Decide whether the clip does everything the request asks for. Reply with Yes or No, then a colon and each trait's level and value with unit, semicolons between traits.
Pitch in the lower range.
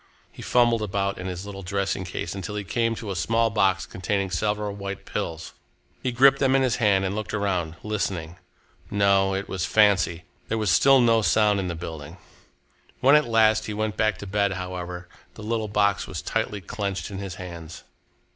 Yes: low, 100 Hz